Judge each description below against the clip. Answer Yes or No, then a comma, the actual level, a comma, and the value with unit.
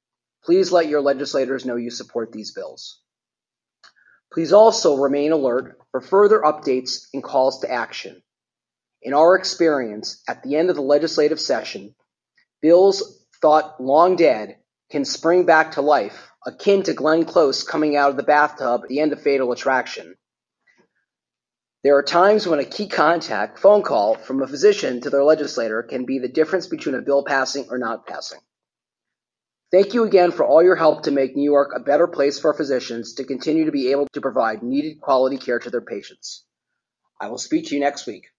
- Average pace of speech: Yes, average, 180 wpm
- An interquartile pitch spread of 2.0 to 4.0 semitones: No, average, 4.4 semitones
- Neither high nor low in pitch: Yes, medium, 150 Hz